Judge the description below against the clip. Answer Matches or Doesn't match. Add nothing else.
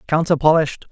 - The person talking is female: Doesn't match